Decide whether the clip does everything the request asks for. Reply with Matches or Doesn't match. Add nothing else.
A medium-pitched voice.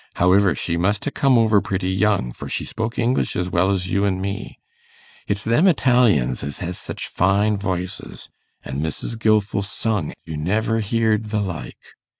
Doesn't match